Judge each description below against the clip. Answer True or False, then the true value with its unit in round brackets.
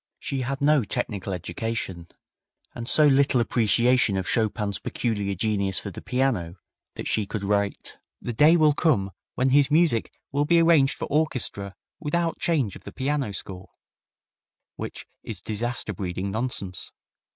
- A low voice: True (115 Hz)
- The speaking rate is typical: True (150 wpm)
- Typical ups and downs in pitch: False (6.0 semitones)